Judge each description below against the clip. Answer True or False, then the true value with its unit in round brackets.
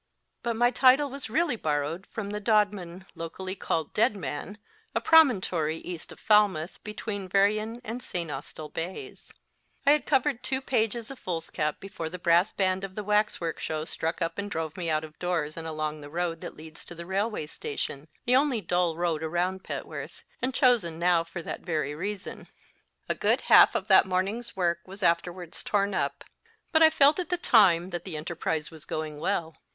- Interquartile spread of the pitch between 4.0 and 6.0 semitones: True (4.8 semitones)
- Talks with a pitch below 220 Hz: True (185 Hz)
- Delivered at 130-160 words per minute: False (190 wpm)